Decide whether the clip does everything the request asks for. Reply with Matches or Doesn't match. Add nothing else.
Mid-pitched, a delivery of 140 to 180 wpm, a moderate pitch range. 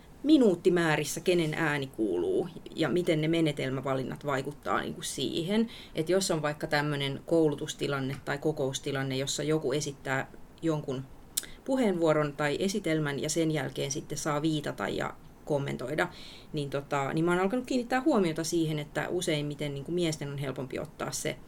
Matches